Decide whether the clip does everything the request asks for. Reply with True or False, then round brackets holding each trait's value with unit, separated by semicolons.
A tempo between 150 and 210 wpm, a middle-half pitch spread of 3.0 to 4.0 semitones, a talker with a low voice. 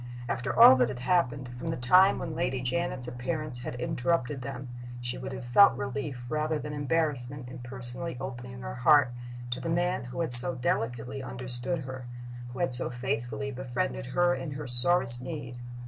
True (180 wpm; 3.5 semitones; 130 Hz)